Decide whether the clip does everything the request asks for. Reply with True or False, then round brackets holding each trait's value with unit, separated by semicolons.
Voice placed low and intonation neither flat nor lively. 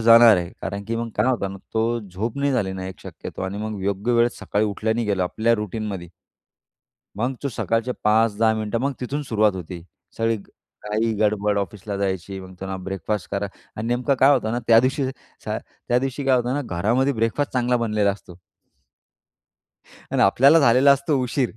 True (110 Hz; 3.5 semitones)